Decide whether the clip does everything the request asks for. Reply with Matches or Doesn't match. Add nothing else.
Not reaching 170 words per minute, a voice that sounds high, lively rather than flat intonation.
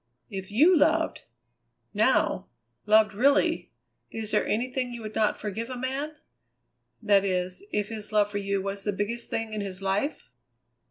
Doesn't match